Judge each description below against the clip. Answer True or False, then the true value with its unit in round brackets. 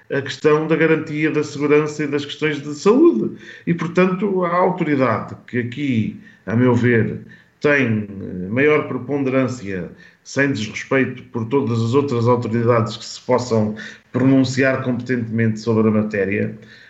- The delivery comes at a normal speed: True (135 wpm)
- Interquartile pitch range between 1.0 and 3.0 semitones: False (4.5 semitones)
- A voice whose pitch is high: False (130 Hz)